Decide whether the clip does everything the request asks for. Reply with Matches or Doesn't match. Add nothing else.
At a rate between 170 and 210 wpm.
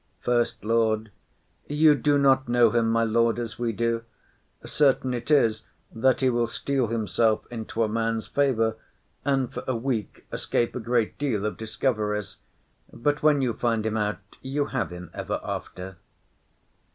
Doesn't match